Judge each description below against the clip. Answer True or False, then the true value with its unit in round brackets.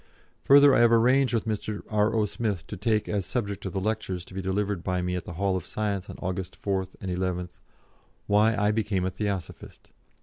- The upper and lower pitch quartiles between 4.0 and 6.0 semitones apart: False (2.7 semitones)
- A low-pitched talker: True (100 Hz)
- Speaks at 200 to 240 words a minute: True (205 wpm)